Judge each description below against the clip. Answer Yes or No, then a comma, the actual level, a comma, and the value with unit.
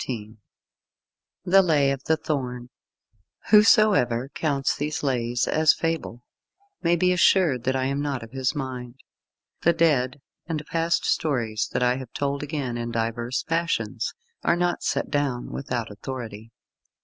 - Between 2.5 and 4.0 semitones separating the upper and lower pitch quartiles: No, average, 4.6 semitones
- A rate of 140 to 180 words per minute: Yes, average, 145 wpm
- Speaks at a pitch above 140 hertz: No, low, 135 Hz